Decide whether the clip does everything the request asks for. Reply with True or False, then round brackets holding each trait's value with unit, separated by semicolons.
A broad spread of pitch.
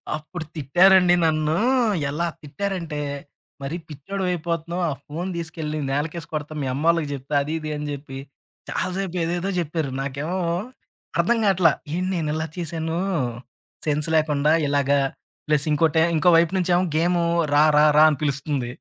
False (2.8 semitones)